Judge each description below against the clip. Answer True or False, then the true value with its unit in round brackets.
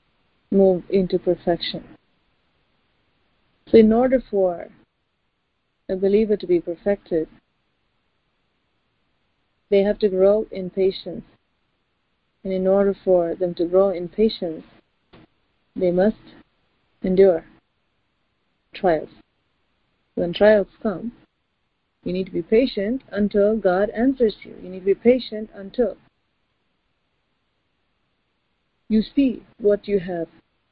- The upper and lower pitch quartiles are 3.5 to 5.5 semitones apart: False (2.8 semitones)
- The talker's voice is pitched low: False (195 Hz)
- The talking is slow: True (105 wpm)